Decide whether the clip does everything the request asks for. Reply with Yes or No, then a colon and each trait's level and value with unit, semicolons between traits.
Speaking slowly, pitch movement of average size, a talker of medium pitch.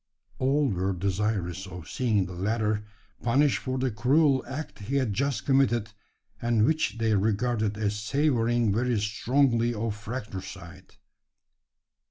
No: slow, 130 wpm; average, 4.1 semitones; low, 110 Hz